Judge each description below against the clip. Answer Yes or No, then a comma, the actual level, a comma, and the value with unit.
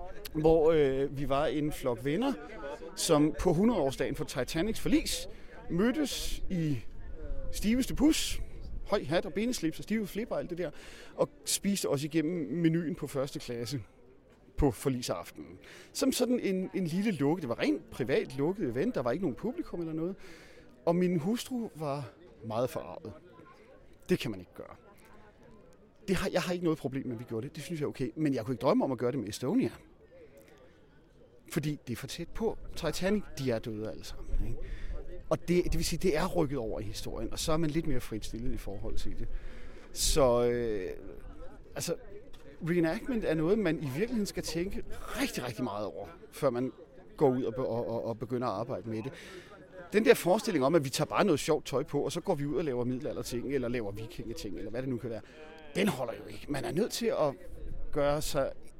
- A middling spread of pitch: No, wide, 6.6 semitones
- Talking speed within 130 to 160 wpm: No, average, 200 wpm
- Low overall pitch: No, medium, 155 Hz